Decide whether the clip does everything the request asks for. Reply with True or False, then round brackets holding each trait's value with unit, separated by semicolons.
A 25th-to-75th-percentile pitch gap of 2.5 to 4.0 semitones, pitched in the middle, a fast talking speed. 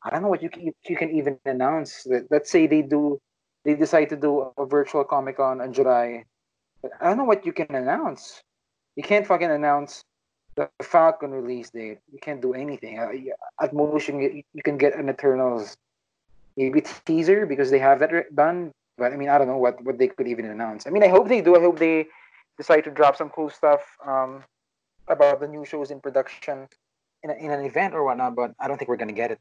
True (2.9 semitones; 145 Hz; 215 wpm)